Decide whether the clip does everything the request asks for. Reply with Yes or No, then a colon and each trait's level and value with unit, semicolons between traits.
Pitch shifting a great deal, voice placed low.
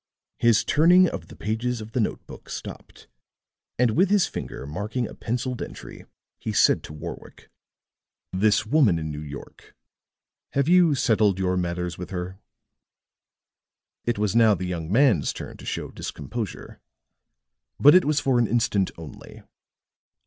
Yes: wide, 6.0 semitones; low, 110 Hz